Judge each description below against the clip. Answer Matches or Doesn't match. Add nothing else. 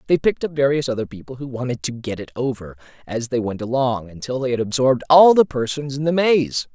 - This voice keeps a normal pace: Doesn't match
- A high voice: Doesn't match